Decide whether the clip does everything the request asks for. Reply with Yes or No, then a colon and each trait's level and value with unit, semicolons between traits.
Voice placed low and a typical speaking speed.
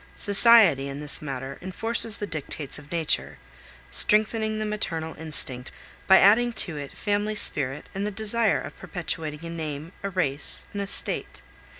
No: medium, 175 Hz; average, 155 wpm